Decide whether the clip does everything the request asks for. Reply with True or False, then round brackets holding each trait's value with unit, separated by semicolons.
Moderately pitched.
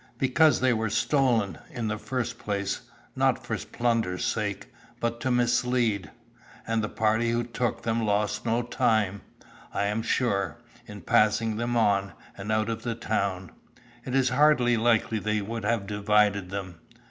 False (110 Hz)